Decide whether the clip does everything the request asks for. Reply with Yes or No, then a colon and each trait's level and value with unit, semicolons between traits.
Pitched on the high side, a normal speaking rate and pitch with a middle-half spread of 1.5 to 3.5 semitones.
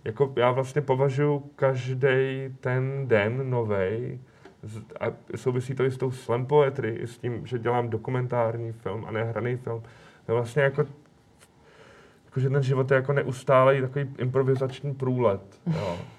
No: low, 130 Hz; average, 150 wpm; narrow, 2.5 semitones